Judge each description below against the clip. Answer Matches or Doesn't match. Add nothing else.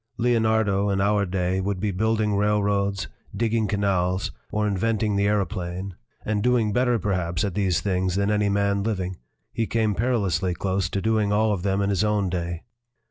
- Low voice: Matches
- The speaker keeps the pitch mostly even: Matches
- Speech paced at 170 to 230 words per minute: Matches